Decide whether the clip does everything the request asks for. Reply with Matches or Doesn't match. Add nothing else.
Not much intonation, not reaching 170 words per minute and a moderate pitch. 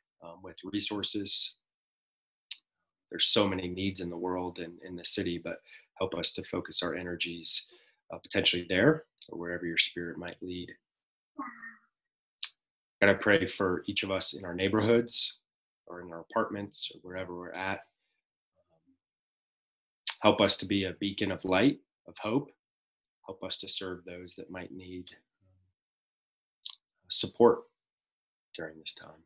Doesn't match